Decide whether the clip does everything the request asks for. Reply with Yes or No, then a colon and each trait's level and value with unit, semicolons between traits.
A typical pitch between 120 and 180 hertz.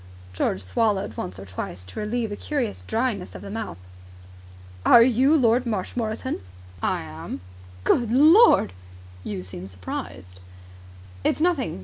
No: high, 215 Hz